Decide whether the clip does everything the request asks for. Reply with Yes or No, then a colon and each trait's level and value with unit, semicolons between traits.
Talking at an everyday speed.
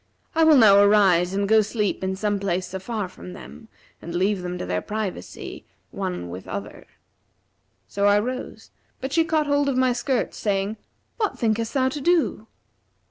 Yes: average, 175 wpm